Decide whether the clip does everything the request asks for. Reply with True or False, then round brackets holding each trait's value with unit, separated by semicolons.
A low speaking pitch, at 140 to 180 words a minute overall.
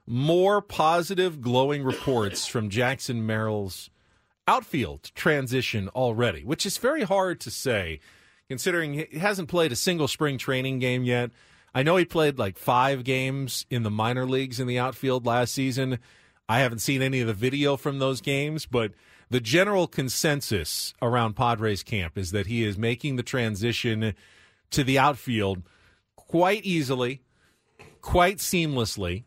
True (130 Hz; 150 wpm)